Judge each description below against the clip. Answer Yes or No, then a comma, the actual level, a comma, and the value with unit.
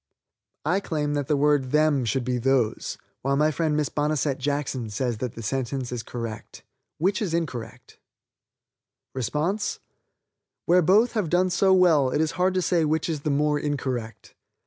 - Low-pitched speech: No, medium, 145 Hz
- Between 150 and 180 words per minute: Yes, average, 165 wpm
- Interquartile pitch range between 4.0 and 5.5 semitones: Yes, average, 4.3 semitones